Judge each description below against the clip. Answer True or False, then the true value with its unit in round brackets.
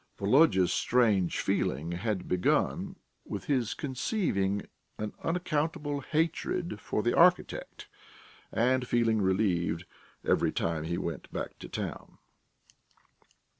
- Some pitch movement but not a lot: False (7.8 semitones)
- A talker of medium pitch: False (110 Hz)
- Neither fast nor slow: False (105 wpm)